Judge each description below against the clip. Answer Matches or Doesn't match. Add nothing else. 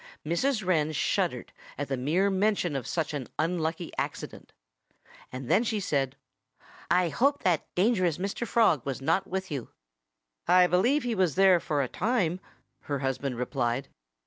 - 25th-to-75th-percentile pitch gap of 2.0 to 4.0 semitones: Doesn't match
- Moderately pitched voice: Matches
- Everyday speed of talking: Matches